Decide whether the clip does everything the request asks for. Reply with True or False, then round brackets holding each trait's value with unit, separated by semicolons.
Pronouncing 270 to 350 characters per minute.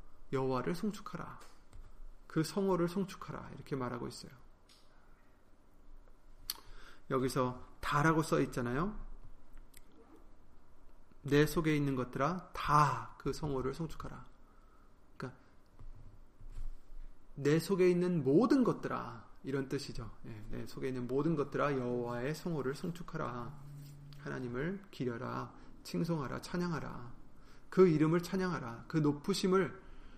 False (240 characters per minute)